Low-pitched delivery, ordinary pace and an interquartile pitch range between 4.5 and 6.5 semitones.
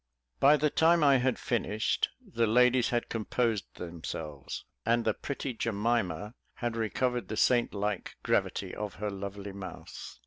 No: low, 115 Hz; average, 145 wpm; average, 3.7 semitones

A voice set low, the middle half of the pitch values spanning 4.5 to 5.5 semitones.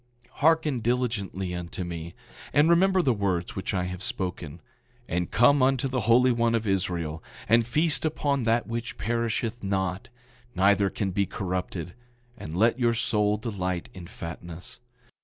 Yes: low, 105 Hz; average, 5.0 semitones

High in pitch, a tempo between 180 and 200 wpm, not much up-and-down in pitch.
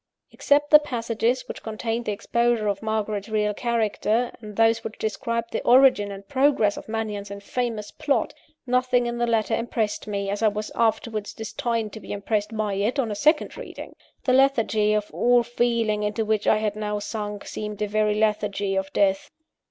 Yes: high, 220 Hz; average, 185 wpm; narrow, 2.2 semitones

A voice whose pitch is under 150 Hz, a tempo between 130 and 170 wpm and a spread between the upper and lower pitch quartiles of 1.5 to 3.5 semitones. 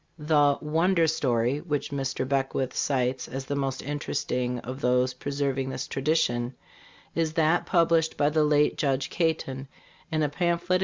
Yes: medium, 140 Hz; average, 150 wpm; average, 3.2 semitones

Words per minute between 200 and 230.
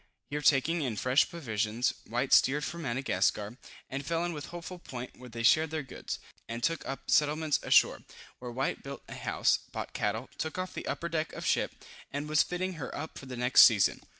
Yes: fast, 205 wpm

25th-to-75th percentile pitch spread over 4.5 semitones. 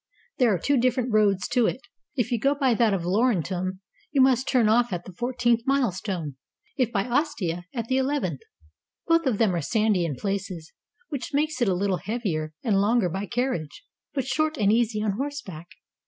Yes: wide, 5.4 semitones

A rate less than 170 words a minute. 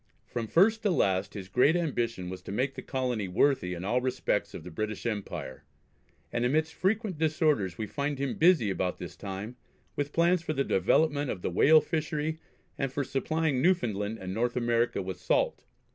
No: average, 185 wpm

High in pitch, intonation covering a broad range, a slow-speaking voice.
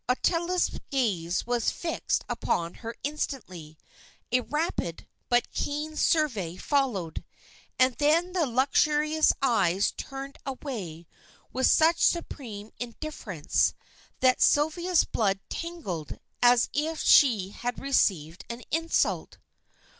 Yes: very high, 255 Hz; wide, 7.3 semitones; slow, 105 wpm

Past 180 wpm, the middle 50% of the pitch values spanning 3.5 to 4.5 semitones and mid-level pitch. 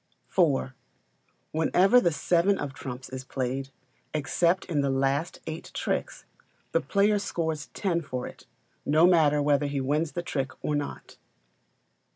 No: average, 145 wpm; average, 4.1 semitones; medium, 150 Hz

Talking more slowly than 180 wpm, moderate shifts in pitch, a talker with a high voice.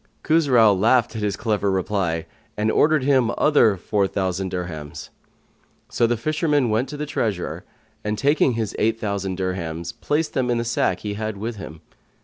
No: average, 170 wpm; average, 4.6 semitones; low, 110 Hz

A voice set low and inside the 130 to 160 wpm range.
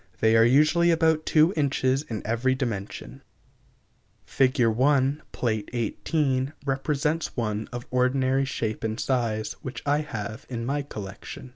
Yes: low, 130 Hz; slow, 135 wpm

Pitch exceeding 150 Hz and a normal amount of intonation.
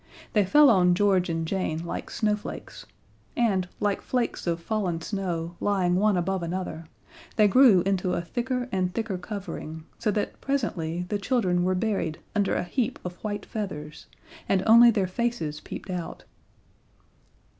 Yes: high, 190 Hz; average, 3.5 semitones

